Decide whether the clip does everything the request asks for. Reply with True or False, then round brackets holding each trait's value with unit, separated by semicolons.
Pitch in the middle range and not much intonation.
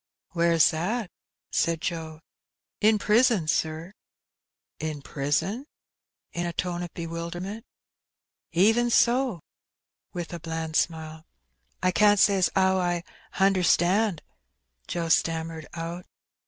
False (175 Hz; 3.3 semitones)